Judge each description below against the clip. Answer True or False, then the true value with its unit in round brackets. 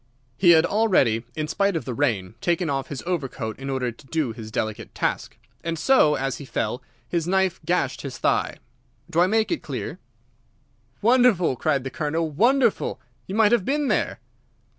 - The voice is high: False (160 Hz)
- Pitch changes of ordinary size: False (6.3 semitones)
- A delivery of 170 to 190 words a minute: True (180 wpm)